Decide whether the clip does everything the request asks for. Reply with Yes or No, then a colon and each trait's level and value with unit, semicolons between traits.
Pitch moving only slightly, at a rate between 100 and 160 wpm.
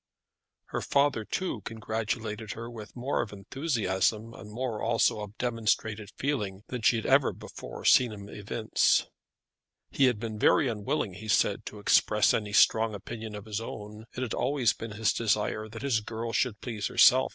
No: narrow, 2.1 semitones; average, 175 wpm